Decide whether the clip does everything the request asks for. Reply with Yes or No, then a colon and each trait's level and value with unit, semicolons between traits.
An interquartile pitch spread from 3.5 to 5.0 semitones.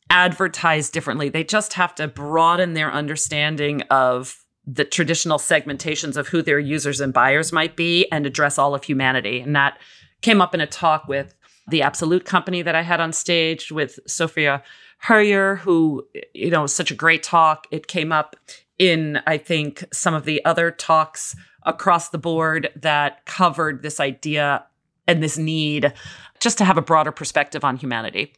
No: average, 2.7 semitones